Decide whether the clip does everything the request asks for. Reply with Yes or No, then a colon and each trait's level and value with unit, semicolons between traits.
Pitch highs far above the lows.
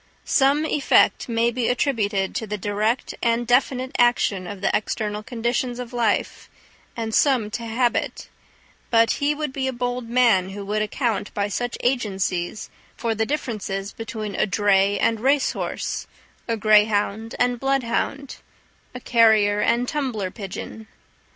No: average, 3.1 semitones